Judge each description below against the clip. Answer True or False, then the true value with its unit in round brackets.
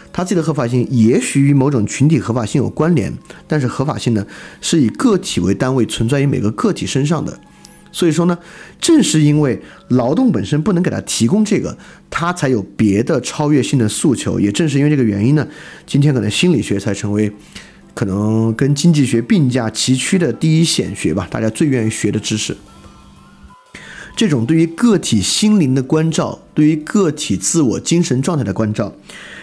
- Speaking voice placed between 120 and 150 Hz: True (140 Hz)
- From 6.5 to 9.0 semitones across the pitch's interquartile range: True (7.0 semitones)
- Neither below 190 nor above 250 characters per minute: False (290 characters per minute)